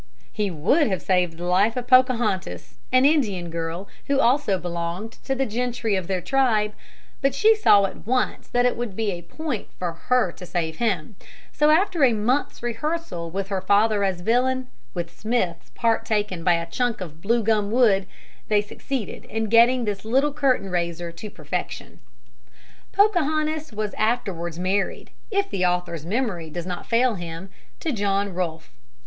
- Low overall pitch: No, high, 210 Hz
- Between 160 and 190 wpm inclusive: Yes, average, 170 wpm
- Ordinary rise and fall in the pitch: No, wide, 5.9 semitones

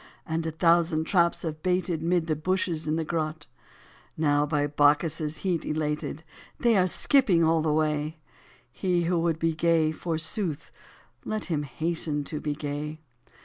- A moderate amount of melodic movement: No, narrow, 2.0 semitones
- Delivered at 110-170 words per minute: Yes, average, 155 wpm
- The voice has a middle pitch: Yes, medium, 160 Hz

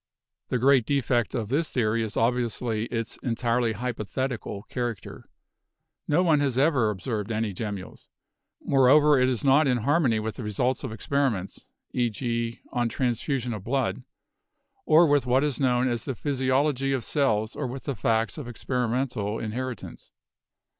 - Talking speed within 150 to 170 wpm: Yes, average, 160 wpm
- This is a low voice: Yes, low, 125 Hz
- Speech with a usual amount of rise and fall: Yes, average, 3.2 semitones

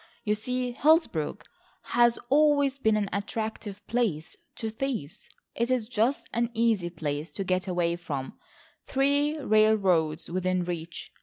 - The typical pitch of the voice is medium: No, high, 215 Hz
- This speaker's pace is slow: Yes, slow, 130 wpm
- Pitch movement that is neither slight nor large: No, wide, 6.0 semitones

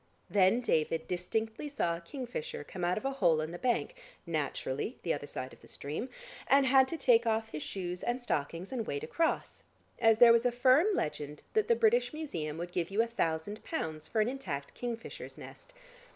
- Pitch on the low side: No, high, 220 Hz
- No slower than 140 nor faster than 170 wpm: No, average, 200 wpm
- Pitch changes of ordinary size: No, wide, 7.7 semitones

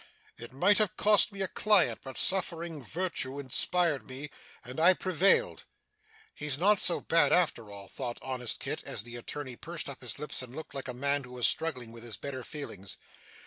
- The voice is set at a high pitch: No, medium, 140 Hz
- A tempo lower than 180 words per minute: No, average, 190 wpm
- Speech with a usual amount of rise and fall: No, wide, 5.7 semitones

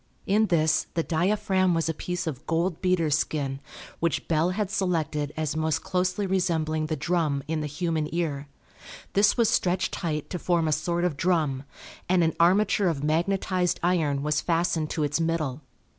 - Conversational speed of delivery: Yes, average, 175 wpm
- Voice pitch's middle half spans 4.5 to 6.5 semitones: No, average, 2.8 semitones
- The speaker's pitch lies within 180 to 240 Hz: No, medium, 165 Hz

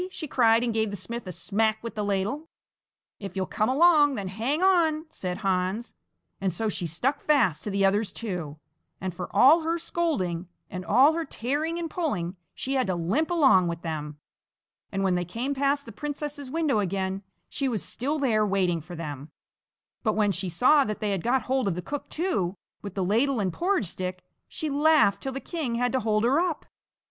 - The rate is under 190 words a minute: No, fast, 205 wpm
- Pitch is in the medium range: No, high, 220 Hz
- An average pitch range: No, wide, 7.2 semitones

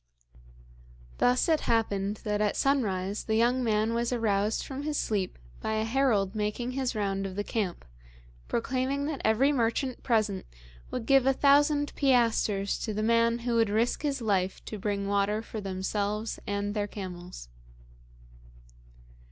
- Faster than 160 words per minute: No, average, 150 wpm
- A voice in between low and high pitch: No, high, 220 Hz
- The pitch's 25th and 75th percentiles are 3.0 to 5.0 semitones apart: Yes, average, 3.7 semitones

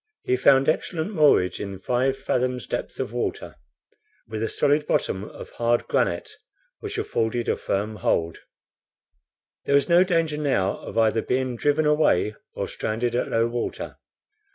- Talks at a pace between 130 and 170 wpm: Yes, average, 155 wpm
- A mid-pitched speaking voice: No, low, 125 Hz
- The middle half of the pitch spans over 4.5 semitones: Yes, average, 4.9 semitones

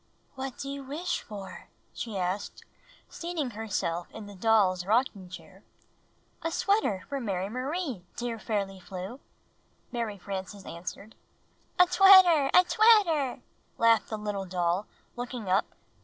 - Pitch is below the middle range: No, high, 220 Hz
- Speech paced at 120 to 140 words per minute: Yes, slow, 135 wpm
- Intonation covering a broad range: Yes, wide, 6.3 semitones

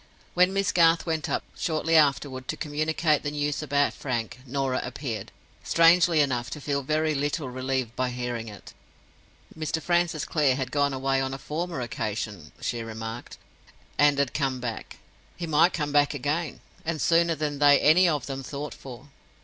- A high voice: No, medium, 145 Hz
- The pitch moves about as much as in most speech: Yes, average, 3.4 semitones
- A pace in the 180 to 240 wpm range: No, average, 170 wpm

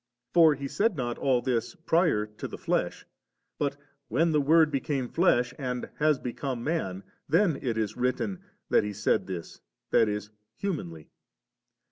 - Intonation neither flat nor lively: No, wide, 6.2 semitones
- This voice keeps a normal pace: Yes, average, 160 wpm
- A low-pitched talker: Yes, low, 130 Hz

